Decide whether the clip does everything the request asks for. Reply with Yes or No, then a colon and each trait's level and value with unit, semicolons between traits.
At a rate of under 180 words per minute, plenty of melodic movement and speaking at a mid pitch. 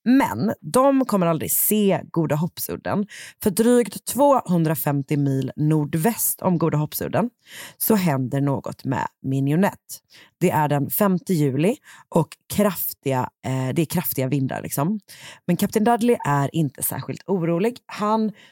Yes: average, 130 wpm; wide, 7.0 semitones; medium, 170 Hz